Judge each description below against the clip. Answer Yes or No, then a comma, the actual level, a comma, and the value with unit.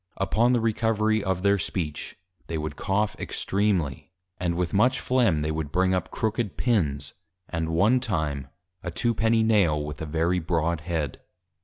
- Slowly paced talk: No, average, 165 wpm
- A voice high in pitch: No, very low, 90 Hz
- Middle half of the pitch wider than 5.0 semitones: Yes, wide, 5.5 semitones